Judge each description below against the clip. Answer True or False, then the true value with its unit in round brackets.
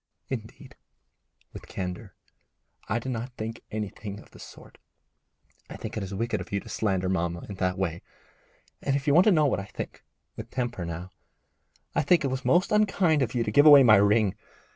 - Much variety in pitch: True (6.2 semitones)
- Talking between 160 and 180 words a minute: False (200 wpm)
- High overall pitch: False (110 Hz)